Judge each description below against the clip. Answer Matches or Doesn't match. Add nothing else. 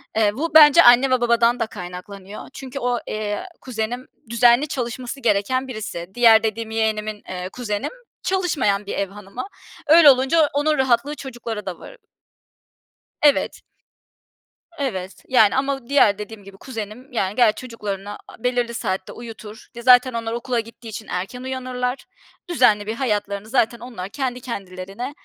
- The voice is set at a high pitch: Matches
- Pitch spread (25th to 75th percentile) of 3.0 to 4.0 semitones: Matches